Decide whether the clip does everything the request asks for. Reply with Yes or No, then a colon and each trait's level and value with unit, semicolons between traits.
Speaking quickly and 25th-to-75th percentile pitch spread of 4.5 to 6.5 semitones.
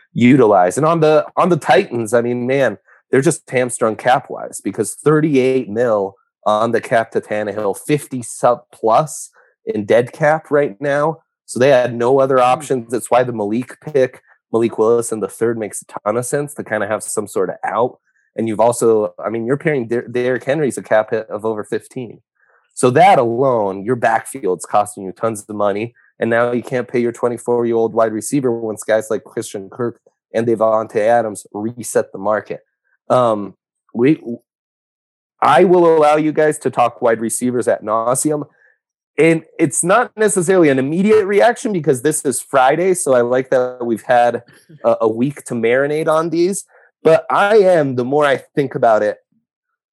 No: average, 185 wpm; average, 4.9 semitones